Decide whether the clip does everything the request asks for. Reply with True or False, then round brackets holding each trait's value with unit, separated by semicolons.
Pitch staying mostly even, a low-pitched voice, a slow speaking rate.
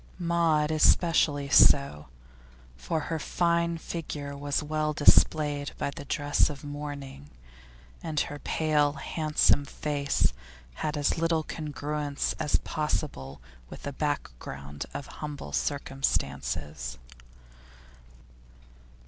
False (1.7 semitones; 145 Hz; 100 wpm)